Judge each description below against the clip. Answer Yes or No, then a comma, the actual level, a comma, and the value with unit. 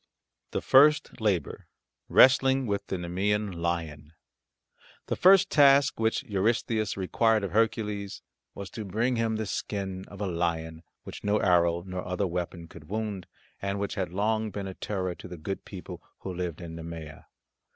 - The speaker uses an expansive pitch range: No, average, 3.9 semitones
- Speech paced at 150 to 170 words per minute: Yes, average, 160 wpm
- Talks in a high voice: No, low, 100 Hz